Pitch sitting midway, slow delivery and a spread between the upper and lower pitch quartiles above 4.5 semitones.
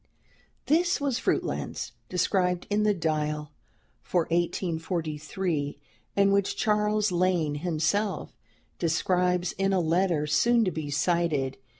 No: medium, 180 Hz; slow, 110 wpm; average, 4.0 semitones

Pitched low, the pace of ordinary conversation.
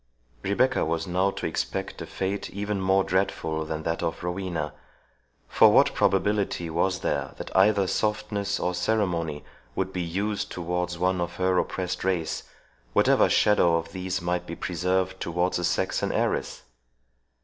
Yes: very low, 90 Hz; average, 150 wpm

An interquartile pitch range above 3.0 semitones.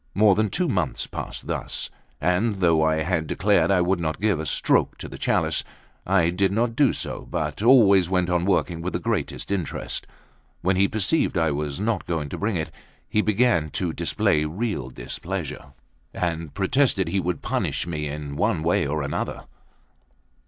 Yes: average, 4.3 semitones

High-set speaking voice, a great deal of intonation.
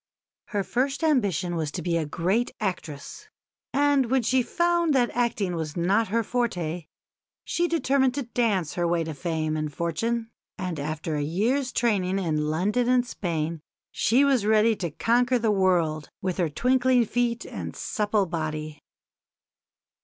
Yes: high, 200 Hz; wide, 6.7 semitones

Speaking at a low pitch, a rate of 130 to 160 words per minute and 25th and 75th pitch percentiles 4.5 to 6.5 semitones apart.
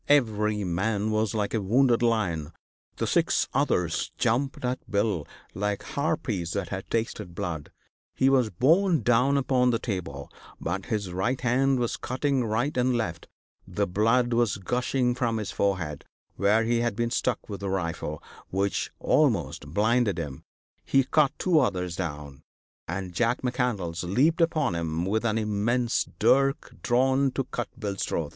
Yes: low, 110 Hz; average, 155 wpm; average, 4.9 semitones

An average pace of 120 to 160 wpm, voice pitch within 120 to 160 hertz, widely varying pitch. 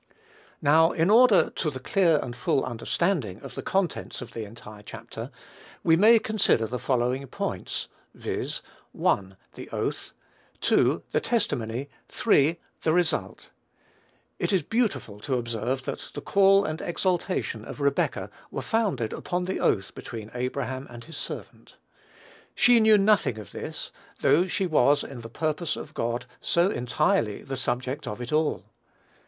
Yes: average, 150 wpm; medium, 140 Hz; wide, 7.2 semitones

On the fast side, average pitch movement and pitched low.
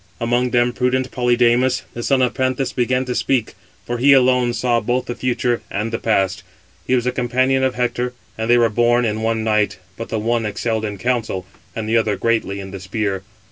No: fast, 210 wpm; narrow, 2.1 semitones; low, 120 Hz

